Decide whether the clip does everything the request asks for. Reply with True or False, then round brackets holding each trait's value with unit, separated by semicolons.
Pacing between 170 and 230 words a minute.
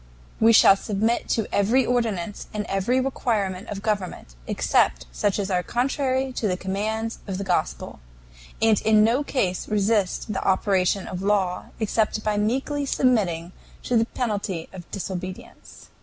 False (150 wpm)